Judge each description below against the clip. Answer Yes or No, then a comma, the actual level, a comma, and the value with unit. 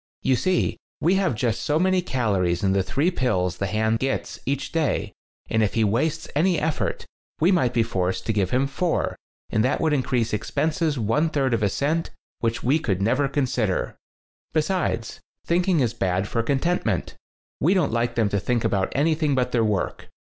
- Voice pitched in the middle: No, low, 125 Hz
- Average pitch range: No, wide, 6.3 semitones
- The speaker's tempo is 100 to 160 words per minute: No, average, 190 wpm